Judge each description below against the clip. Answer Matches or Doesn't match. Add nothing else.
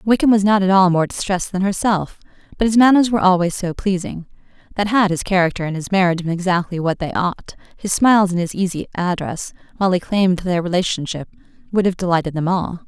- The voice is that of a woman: Matches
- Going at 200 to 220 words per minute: Matches